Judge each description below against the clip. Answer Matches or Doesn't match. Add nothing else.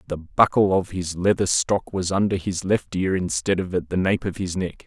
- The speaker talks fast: Matches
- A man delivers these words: Matches